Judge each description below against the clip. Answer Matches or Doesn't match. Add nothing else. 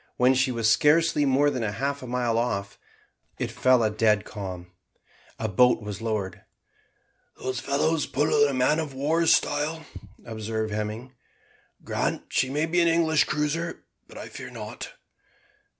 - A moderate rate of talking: Matches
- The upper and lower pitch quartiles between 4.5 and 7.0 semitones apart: Matches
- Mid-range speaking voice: Doesn't match